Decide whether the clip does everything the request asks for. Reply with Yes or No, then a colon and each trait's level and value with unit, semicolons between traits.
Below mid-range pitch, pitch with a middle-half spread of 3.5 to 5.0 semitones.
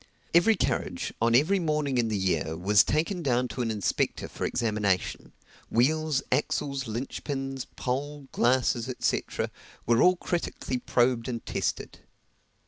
Yes: low, 130 Hz; average, 4.3 semitones